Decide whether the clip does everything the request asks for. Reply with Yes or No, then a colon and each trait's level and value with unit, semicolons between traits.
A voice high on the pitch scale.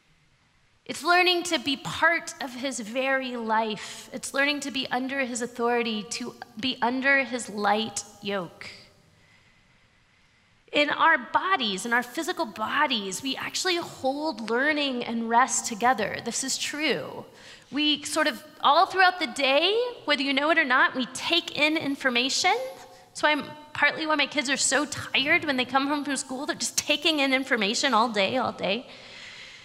Yes: very high, 270 Hz